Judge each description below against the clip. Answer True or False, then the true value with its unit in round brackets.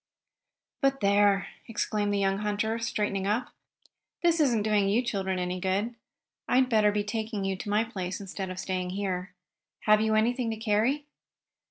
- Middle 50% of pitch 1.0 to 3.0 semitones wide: True (2.4 semitones)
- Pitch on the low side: False (210 Hz)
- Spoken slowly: False (165 wpm)